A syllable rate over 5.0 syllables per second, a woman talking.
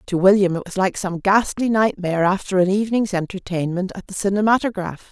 Yes: 5.9 syllables/s; female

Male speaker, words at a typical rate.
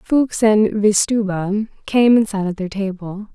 No: female; average, 160 wpm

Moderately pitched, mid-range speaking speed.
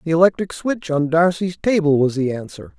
Yes: medium, 165 Hz; average, 195 wpm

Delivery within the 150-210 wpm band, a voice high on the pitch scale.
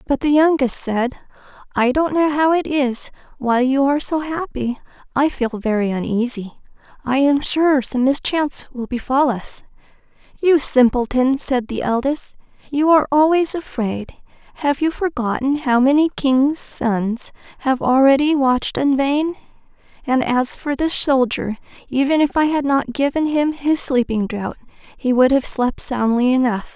Yes: average, 155 wpm; very high, 270 Hz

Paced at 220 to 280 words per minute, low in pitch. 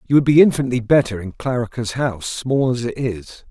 No: fast, 205 wpm; low, 125 Hz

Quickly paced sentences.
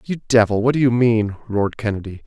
Yes: fast, 210 wpm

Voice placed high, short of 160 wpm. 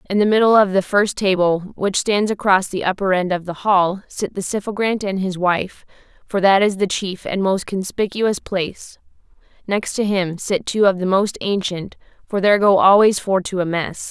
No: high, 195 Hz; fast, 205 wpm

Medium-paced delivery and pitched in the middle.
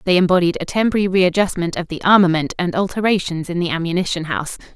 Yes: average, 175 wpm; medium, 180 Hz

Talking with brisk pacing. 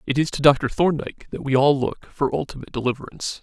Yes: fast, 210 wpm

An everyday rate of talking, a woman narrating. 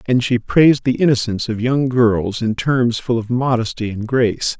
No: average, 195 wpm; male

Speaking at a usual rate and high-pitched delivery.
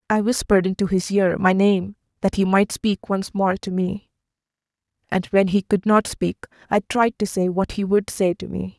No: fast, 210 wpm; high, 195 Hz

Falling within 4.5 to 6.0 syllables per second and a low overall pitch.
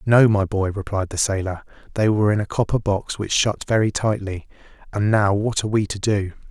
Yes: 5.5 syllables/s; low, 100 Hz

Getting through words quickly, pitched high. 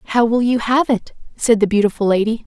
Yes: fast, 210 wpm; high, 225 Hz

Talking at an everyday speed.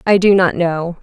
No: fast, 235 wpm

